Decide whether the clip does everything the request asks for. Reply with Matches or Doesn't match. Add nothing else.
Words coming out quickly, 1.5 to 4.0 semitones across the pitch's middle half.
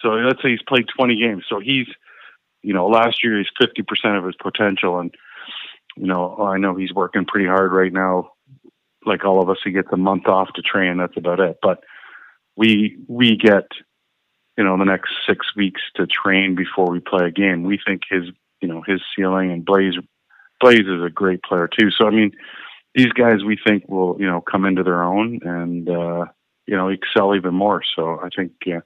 Matches